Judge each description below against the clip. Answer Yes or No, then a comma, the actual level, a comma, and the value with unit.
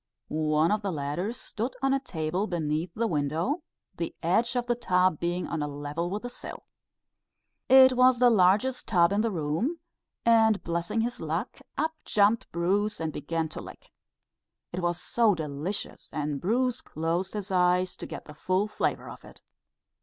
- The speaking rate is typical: Yes, average, 175 wpm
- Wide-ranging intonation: Yes, wide, 5.9 semitones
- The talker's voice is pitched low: No, medium, 185 Hz